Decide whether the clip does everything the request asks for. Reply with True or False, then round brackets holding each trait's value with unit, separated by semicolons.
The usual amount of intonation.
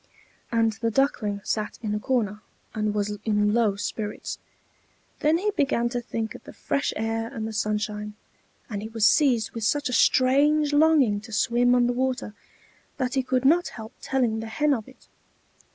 True (3.7 semitones)